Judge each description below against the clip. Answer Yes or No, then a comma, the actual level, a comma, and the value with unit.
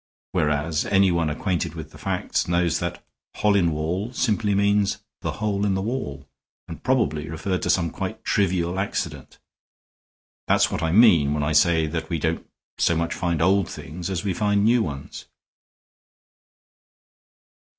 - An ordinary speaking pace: Yes, average, 150 wpm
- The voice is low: Yes, very low, 90 Hz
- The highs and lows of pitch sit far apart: No, average, 4.0 semitones